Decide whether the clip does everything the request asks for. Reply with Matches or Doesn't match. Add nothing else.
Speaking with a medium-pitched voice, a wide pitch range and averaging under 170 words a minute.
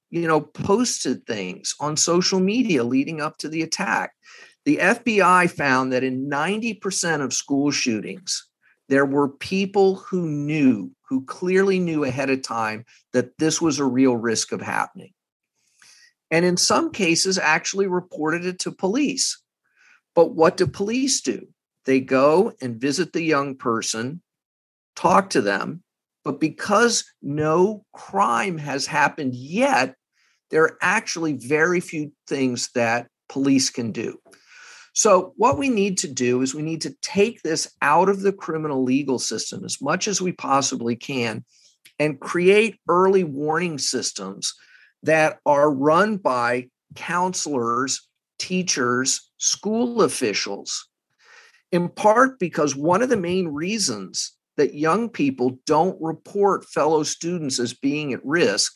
Matches